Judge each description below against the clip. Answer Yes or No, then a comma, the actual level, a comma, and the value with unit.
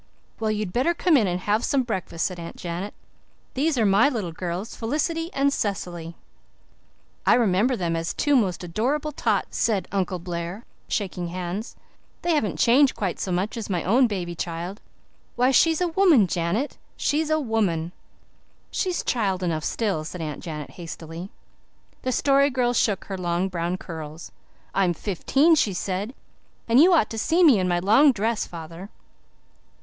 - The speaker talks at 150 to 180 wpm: Yes, average, 165 wpm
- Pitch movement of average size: No, wide, 6.6 semitones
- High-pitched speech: Yes, high, 200 Hz